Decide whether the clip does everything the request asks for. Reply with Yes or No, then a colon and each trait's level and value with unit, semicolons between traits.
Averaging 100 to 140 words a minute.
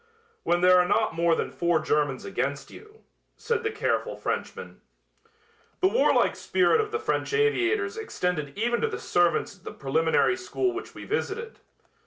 No: average, 165 wpm